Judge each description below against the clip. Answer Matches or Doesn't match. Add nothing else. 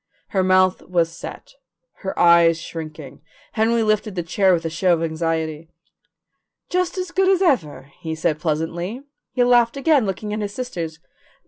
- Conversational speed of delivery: Matches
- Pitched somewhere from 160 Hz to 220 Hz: Matches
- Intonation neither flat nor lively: Doesn't match